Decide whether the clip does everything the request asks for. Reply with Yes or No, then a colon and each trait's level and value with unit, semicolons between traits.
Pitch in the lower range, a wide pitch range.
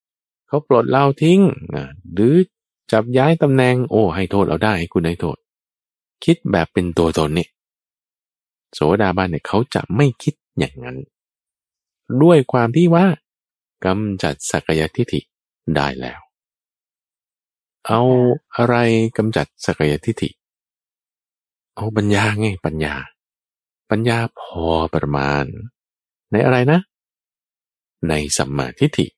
Yes: low, 105 Hz; wide, 8.3 semitones